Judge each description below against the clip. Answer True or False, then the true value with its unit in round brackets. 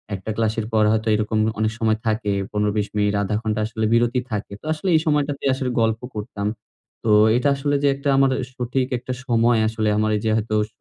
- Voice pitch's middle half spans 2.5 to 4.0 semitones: True (2.9 semitones)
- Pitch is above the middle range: False (110 Hz)